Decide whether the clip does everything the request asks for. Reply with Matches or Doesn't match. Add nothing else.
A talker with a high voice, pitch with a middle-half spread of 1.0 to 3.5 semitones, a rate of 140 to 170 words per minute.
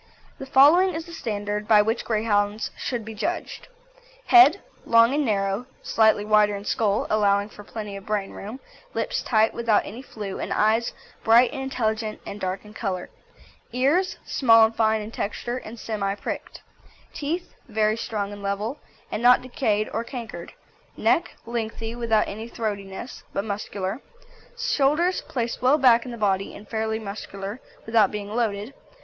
Matches